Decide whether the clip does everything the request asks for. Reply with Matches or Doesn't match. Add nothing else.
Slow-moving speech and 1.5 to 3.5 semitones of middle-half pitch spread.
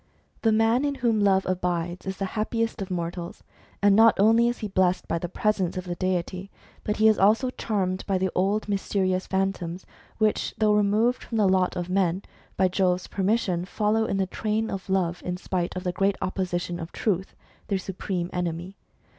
Doesn't match